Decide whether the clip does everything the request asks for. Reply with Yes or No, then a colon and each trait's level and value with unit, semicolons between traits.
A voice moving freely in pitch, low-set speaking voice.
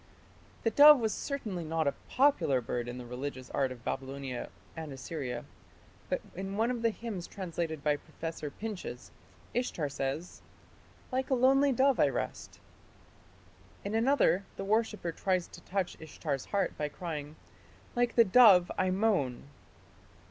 No: wide, 7.9 semitones; medium, 180 Hz